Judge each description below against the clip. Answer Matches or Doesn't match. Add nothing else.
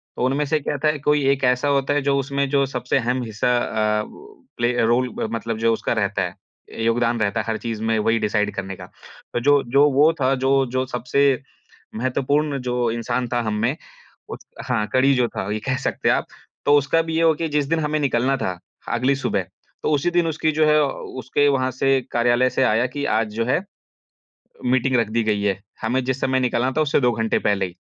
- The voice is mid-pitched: Doesn't match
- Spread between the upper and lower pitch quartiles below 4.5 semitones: Matches